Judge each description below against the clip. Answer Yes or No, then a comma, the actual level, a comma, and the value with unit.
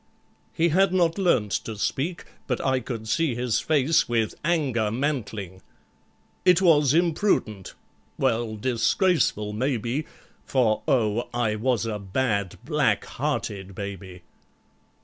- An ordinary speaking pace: No, slow, 115 wpm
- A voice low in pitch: Yes, low, 120 Hz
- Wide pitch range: Yes, wide, 6.1 semitones